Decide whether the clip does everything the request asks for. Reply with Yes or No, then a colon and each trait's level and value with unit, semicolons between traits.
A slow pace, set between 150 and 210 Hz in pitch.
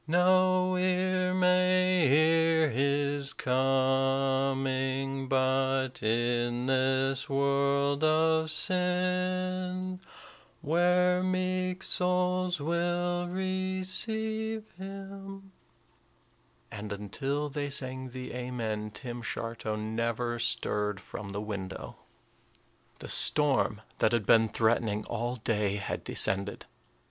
No: slow, 90 wpm; medium, 140 Hz